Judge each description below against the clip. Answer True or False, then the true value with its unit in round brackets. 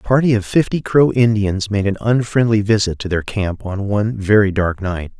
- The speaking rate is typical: False (210 wpm)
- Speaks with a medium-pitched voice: False (105 Hz)